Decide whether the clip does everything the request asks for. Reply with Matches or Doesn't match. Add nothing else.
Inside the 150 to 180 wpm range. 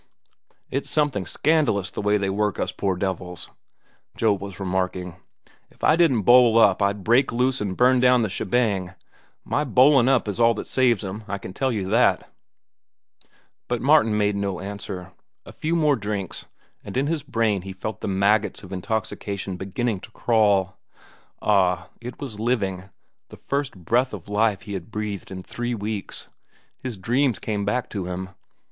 Matches